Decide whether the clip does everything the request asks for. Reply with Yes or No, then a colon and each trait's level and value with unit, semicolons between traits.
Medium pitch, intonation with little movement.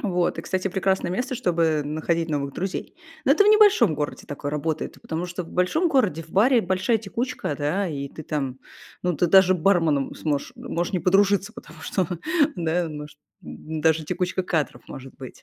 No: medium, 175 Hz; average, 4.2 semitones